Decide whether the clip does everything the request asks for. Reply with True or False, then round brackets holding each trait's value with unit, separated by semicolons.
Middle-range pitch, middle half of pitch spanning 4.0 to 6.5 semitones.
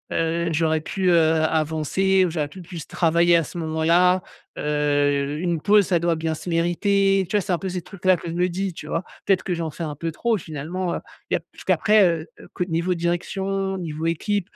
False (170 Hz; 2.8 semitones)